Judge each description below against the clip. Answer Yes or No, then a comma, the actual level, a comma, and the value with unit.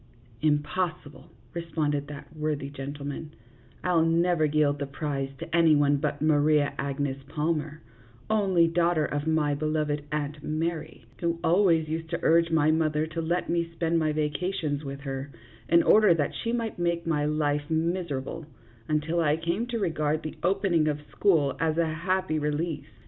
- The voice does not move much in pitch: Yes, narrow, 2.3 semitones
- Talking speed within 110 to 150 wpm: No, average, 170 wpm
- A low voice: No, medium, 155 Hz